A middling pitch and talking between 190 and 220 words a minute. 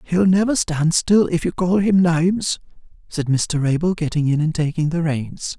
Yes: medium, 165 Hz; average, 195 wpm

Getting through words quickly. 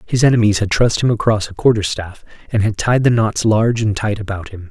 Yes: fast, 240 wpm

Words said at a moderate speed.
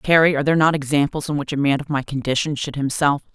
No: fast, 250 wpm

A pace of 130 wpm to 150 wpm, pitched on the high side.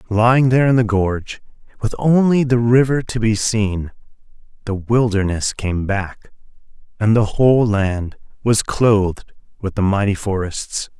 No: average, 140 wpm; low, 110 Hz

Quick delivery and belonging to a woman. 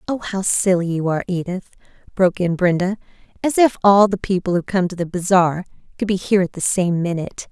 Yes: fast, 210 wpm; female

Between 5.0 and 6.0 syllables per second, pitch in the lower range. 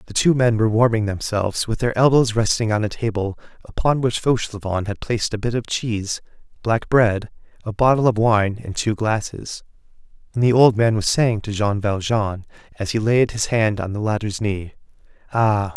Yes: 5.2 syllables/s; low, 110 Hz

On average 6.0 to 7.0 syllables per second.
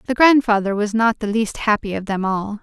No: 5.3 syllables/s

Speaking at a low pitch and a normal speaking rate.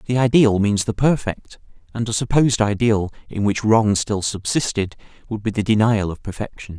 Yes: low, 110 Hz; average, 175 wpm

